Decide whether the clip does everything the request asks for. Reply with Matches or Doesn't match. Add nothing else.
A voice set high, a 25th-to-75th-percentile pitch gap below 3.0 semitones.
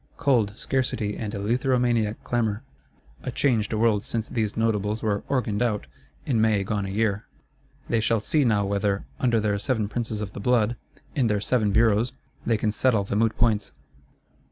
Doesn't match